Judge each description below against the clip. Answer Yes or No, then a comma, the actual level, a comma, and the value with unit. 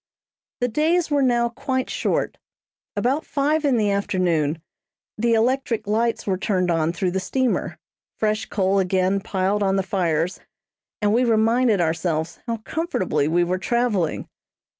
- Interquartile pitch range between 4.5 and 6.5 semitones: Yes, average, 4.9 semitones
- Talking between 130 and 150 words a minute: Yes, average, 145 wpm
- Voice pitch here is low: No, high, 205 Hz